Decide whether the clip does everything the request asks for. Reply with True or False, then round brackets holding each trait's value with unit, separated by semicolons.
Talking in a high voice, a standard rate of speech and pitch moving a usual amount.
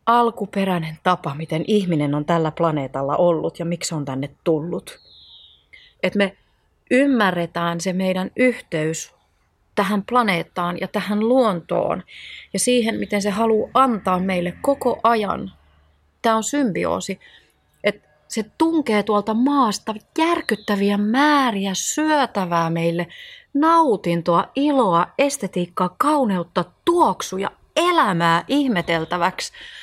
False (195 Hz; 105 wpm; 6.5 semitones)